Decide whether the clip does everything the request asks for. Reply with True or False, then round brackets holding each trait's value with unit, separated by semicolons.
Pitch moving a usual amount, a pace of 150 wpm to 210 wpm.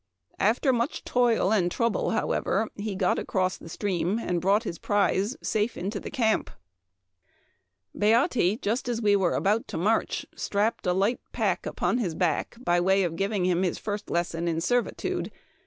True (3.8 semitones; 175 wpm)